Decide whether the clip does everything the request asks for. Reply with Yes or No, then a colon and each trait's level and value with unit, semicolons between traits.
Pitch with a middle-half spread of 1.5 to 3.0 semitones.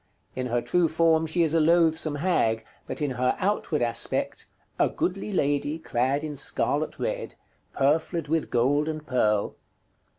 No: average, 4.3 semitones